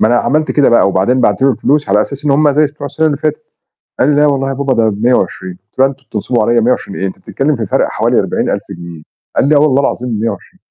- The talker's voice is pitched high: No, low, 130 Hz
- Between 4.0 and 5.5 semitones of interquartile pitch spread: Yes, average, 4.5 semitones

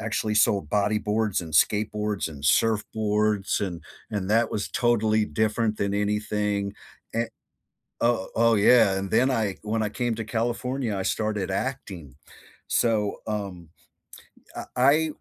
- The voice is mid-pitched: No, low, 105 Hz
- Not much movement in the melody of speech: Yes, narrow, 2.0 semitones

